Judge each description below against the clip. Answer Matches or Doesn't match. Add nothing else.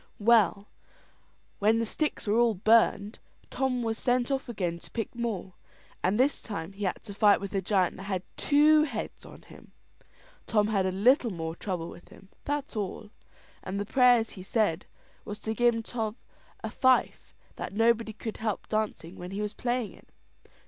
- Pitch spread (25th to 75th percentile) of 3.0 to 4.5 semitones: Matches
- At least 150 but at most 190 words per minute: Matches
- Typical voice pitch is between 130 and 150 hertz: Doesn't match